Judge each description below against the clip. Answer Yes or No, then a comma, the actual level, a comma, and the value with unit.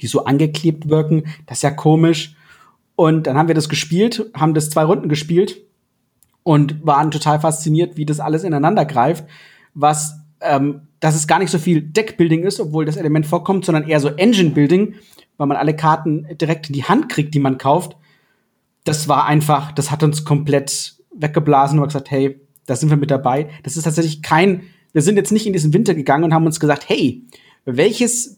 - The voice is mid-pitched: Yes, medium, 155 Hz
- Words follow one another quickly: Yes, fast, 200 wpm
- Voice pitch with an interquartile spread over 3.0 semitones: No, narrow, 2.5 semitones